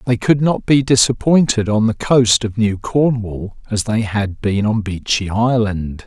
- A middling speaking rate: Yes, average, 180 wpm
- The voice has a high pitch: No, low, 110 Hz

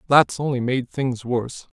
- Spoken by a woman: No, male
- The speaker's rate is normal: Yes, average, 165 wpm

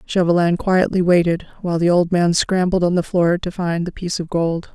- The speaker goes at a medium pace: No, fast, 215 wpm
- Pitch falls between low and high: Yes, medium, 175 Hz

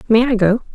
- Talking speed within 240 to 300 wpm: Yes, fast, 245 wpm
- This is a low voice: No, high, 225 Hz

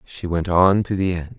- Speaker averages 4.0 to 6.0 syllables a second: Yes, 4.7 syllables/s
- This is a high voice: No, very low, 90 Hz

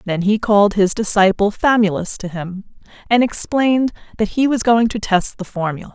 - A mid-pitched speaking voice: No, high, 210 Hz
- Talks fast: No, average, 180 wpm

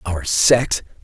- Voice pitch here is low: Yes, low, 105 Hz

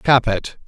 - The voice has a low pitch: Yes, low, 120 Hz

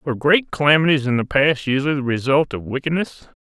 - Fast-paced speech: No, average, 190 wpm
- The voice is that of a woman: No, male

